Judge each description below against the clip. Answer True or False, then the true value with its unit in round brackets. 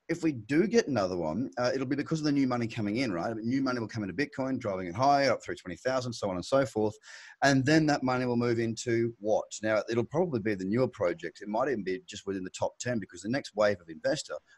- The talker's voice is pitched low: True (120 Hz)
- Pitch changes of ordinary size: True (4.1 semitones)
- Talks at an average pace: False (275 wpm)